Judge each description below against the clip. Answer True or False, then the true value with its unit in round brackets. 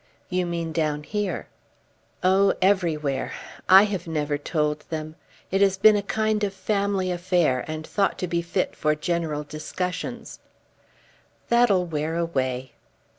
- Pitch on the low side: False (170 Hz)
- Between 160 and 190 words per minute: False (135 wpm)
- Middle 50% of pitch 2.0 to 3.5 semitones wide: False (4.1 semitones)